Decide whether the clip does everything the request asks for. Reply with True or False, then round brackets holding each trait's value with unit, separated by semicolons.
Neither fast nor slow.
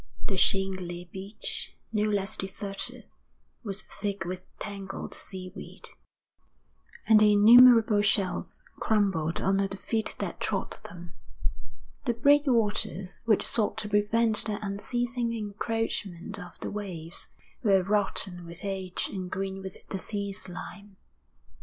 False (120 wpm)